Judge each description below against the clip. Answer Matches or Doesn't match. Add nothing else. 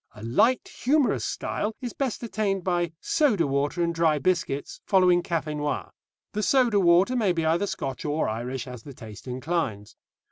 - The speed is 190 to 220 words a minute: Doesn't match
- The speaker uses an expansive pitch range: Matches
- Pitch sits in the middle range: Matches